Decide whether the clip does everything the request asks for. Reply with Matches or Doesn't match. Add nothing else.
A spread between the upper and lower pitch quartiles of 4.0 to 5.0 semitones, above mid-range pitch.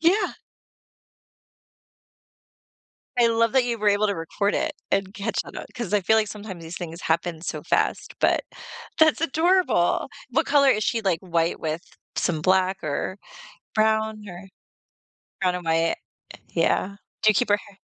Matches